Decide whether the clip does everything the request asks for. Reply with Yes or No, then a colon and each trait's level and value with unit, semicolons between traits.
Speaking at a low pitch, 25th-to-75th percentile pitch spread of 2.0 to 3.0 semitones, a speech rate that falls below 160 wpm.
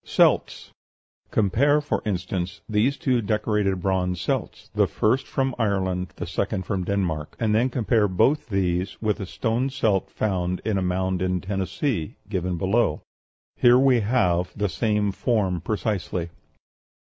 No: low, 100 Hz; average, 3.7 semitones; average, 145 wpm